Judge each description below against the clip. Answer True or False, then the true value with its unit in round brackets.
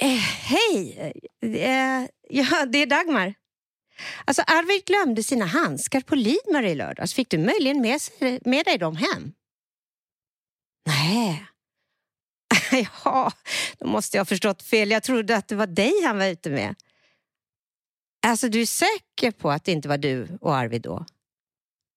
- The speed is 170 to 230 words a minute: False (155 wpm)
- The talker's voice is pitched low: False (250 Hz)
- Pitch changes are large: True (6.6 semitones)